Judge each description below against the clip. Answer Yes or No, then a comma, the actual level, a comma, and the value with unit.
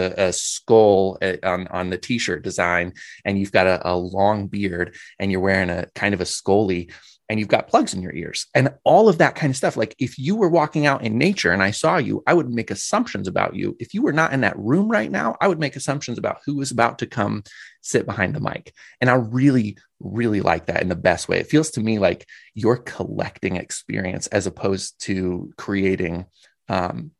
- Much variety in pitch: Yes, wide, 6.2 semitones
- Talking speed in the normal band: No, fast, 225 wpm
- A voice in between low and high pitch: No, low, 105 Hz